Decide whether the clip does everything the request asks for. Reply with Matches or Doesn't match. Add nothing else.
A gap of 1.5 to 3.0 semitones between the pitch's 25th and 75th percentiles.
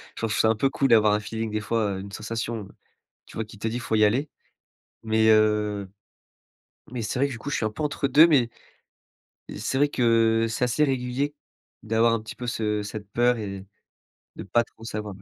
Matches